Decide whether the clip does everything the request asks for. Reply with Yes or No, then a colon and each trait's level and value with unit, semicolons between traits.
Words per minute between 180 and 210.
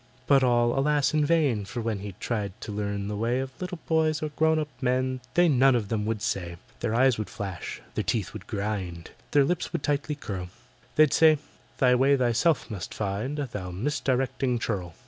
Yes: average, 190 wpm